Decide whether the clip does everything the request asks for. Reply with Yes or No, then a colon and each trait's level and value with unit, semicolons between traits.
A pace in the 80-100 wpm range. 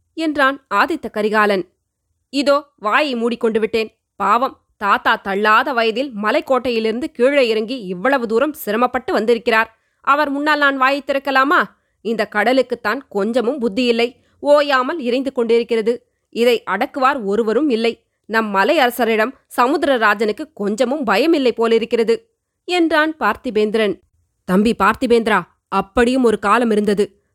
No: average, 110 wpm